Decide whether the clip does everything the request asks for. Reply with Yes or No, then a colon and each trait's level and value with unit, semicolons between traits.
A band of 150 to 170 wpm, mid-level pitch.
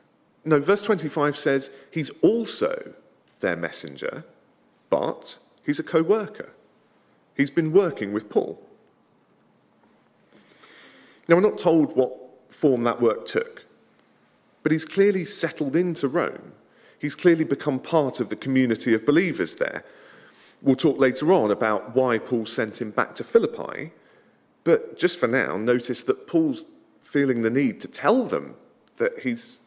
No: average, 140 wpm; medium, 155 Hz